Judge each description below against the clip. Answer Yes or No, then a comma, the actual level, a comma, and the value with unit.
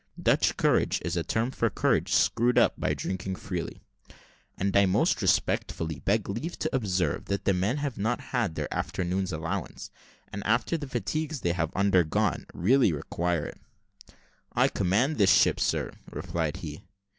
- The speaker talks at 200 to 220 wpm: No, average, 160 wpm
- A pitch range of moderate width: Yes, average, 5.0 semitones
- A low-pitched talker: Yes, very low, 95 Hz